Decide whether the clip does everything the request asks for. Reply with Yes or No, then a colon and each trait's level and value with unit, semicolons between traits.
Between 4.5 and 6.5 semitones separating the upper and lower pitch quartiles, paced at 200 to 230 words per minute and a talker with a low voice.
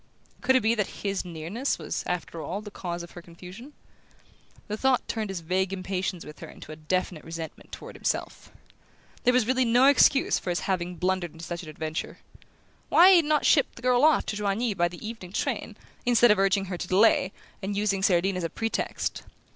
No: average, 4.8 semitones; fast, 205 wpm; high, 195 Hz